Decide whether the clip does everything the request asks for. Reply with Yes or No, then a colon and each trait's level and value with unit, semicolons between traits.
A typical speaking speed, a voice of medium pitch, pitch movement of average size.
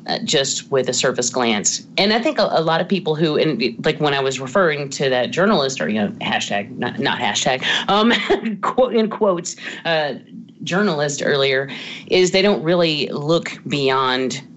No: average, 180 wpm; medium, 165 Hz; wide, 6.8 semitones